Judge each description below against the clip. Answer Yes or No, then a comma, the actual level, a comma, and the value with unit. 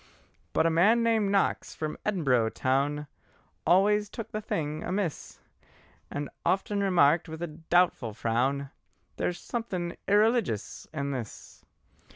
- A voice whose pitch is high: No, medium, 170 Hz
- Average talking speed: No, slow, 130 wpm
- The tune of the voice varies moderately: No, wide, 6.2 semitones